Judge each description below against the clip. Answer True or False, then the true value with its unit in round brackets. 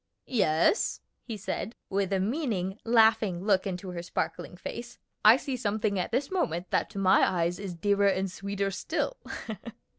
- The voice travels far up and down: False (3.1 semitones)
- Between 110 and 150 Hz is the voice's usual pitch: False (200 Hz)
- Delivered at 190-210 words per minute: False (160 wpm)